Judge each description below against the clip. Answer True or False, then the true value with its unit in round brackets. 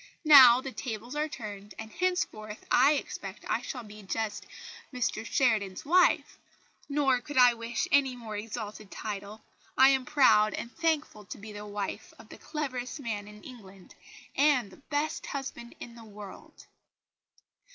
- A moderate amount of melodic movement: True (4.5 semitones)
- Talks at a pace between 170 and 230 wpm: False (155 wpm)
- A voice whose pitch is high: True (235 Hz)